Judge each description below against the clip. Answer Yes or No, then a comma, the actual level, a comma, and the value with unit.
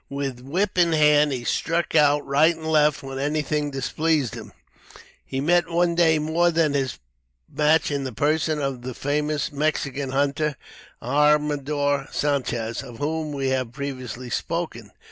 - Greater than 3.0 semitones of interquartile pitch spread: No, narrow, 2.4 semitones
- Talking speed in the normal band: Yes, average, 150 wpm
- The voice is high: No, medium, 145 Hz